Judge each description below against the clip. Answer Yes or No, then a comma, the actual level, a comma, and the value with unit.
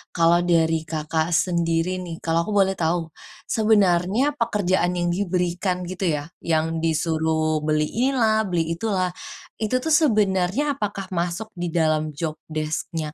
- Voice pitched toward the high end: No, medium, 175 Hz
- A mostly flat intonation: No, average, 3.8 semitones